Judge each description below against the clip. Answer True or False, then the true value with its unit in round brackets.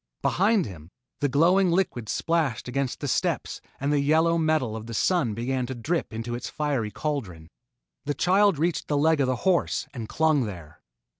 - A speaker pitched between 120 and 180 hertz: True (140 Hz)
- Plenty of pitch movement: True (5.7 semitones)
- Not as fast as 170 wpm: False (180 wpm)